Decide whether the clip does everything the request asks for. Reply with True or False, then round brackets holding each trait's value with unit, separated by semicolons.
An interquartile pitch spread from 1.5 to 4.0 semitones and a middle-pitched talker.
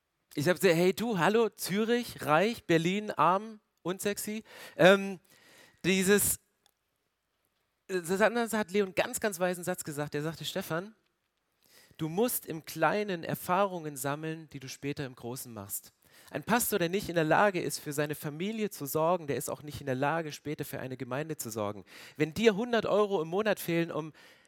False (5.4 semitones; 175 Hz)